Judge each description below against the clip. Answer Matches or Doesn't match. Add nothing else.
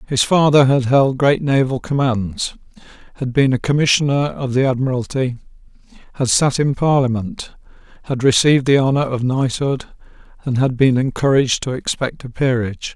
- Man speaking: Matches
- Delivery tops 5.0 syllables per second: Matches